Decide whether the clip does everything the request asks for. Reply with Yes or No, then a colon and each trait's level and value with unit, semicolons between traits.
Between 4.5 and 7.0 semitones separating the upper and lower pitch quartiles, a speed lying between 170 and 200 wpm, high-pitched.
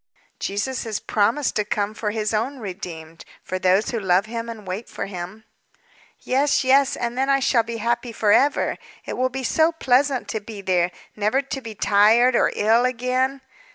No: average, 3.9 semitones; average, 185 wpm; high, 230 Hz